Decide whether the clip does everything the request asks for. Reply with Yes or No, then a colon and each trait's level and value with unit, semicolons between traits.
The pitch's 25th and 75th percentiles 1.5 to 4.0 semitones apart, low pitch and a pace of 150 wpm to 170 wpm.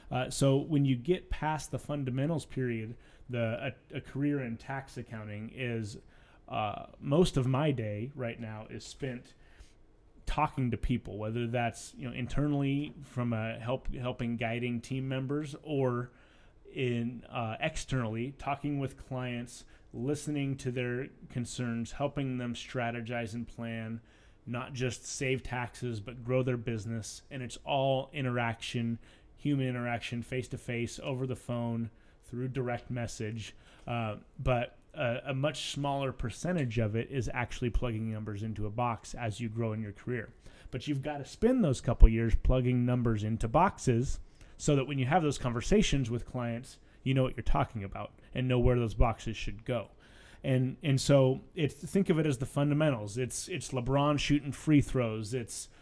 Yes: average, 2.8 semitones; low, 125 Hz; average, 165 wpm